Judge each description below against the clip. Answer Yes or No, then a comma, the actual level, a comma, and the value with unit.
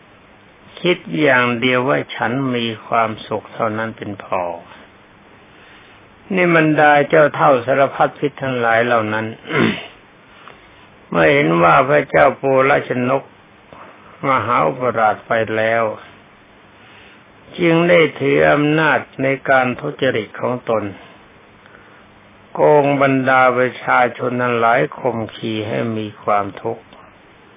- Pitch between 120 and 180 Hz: Yes, low, 125 Hz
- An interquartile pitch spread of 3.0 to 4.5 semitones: Yes, average, 3.9 semitones